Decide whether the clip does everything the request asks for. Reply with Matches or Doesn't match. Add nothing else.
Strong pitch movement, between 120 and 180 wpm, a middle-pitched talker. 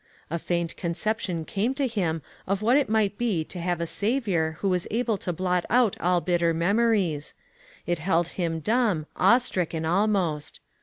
Doesn't match